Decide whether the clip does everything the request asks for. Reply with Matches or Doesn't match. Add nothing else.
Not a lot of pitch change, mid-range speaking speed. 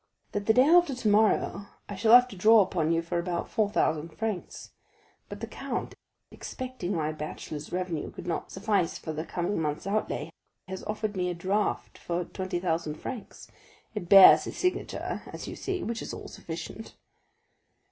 Doesn't match